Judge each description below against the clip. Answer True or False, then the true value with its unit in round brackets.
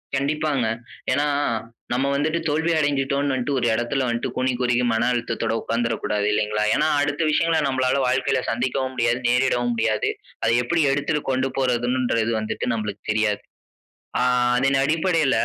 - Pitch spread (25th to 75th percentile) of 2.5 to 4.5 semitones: True (3.4 semitones)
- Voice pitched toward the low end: True (130 Hz)